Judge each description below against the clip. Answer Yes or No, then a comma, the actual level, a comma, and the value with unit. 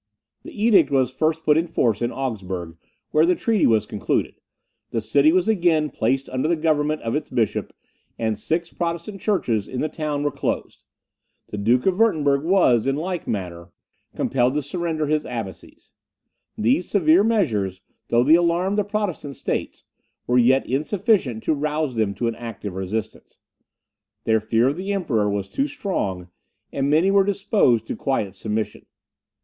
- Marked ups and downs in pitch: Yes, wide, 7.2 semitones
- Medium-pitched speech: Yes, medium, 145 Hz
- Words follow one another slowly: No, average, 165 wpm